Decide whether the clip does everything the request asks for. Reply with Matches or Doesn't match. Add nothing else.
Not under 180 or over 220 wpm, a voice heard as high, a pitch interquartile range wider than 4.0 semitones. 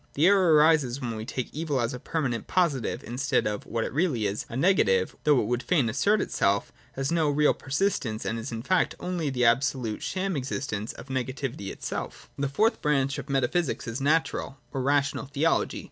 Doesn't match